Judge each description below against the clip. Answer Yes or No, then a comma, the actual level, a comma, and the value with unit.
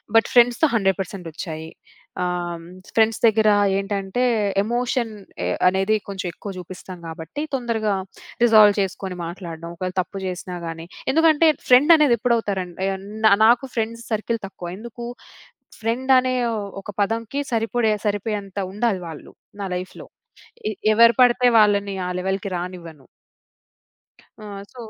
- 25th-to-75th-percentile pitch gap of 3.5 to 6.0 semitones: Yes, average, 4.2 semitones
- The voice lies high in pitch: Yes, high, 205 Hz